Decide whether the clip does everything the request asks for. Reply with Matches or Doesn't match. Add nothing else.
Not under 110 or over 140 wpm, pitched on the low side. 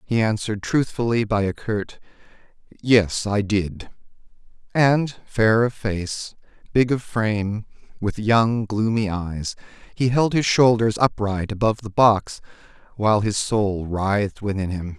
Matches